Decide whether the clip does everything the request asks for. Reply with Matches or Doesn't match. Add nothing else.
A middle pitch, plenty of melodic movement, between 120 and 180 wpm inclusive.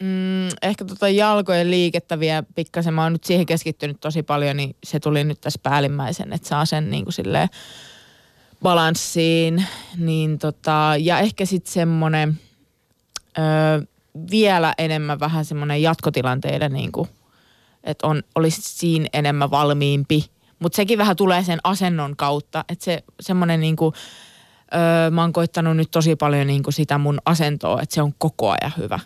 Doesn't match